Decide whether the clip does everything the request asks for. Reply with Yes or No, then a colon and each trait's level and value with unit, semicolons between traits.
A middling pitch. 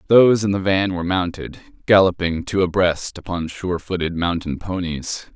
No: very low, 90 Hz